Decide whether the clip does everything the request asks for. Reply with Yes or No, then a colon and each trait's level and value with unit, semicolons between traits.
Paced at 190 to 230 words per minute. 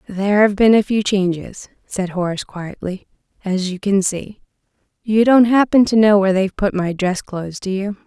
Yes: average, 195 wpm